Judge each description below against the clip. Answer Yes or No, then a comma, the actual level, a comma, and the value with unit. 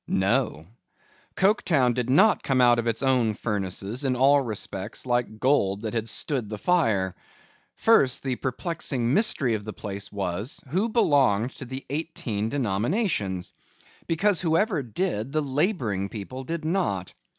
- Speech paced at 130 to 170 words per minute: Yes, average, 145 wpm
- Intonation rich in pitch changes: Yes, wide, 6.5 semitones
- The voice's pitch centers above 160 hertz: No, low, 125 Hz